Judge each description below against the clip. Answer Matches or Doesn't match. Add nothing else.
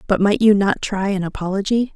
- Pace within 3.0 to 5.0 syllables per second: Doesn't match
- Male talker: Doesn't match